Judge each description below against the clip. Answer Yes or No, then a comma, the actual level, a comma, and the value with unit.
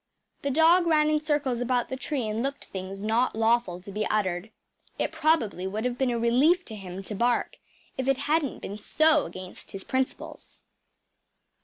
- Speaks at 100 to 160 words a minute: No, average, 180 wpm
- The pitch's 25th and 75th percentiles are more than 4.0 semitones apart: Yes, wide, 5.6 semitones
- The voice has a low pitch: No, high, 245 Hz